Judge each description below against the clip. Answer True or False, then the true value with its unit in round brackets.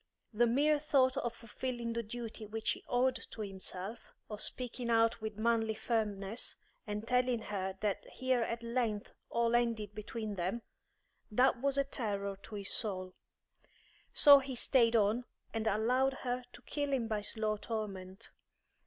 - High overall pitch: True (230 Hz)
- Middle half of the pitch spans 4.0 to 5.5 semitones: False (2.8 semitones)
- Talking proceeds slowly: False (155 wpm)